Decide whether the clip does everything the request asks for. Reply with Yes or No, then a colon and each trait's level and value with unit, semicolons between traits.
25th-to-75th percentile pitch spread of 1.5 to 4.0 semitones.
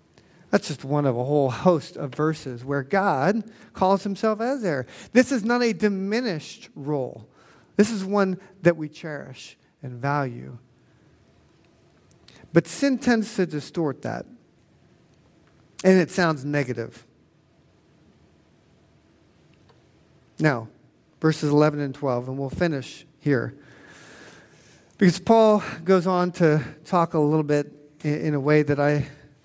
No: average, 4.7 semitones